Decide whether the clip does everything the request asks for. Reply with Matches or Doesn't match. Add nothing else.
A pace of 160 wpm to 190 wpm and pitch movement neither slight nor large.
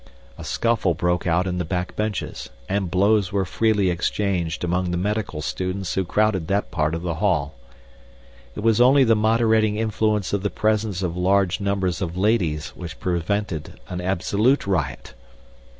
Matches